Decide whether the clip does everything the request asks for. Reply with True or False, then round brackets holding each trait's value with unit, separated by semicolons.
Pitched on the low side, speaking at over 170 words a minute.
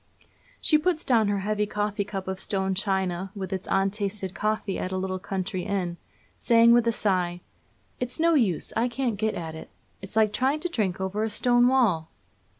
False (205 Hz; 190 wpm)